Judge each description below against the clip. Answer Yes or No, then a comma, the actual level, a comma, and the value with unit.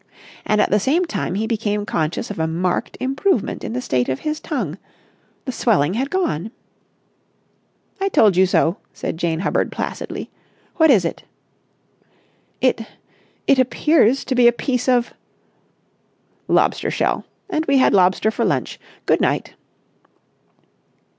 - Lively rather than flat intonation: Yes, wide, 6.5 semitones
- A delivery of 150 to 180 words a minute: No, average, 140 wpm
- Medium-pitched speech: No, high, 225 Hz